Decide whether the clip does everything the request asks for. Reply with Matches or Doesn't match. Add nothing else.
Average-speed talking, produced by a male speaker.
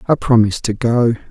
Matches